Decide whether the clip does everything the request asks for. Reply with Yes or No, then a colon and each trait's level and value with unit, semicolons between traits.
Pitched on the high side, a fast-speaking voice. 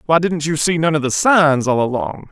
No: medium, 155 Hz; fast, 260 wpm